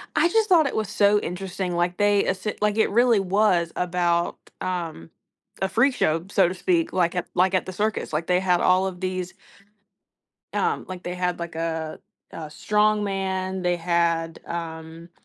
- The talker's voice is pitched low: No, medium, 185 Hz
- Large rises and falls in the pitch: No, average, 3.1 semitones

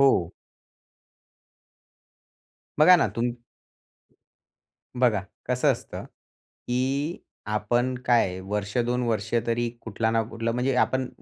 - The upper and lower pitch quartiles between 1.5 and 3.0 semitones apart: Yes, narrow, 2.5 semitones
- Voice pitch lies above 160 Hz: No, low, 120 Hz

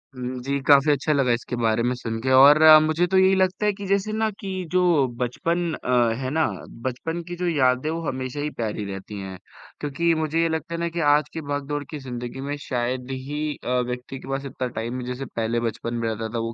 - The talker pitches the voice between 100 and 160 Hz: Yes, low, 135 Hz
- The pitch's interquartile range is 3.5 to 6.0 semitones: Yes, average, 4.6 semitones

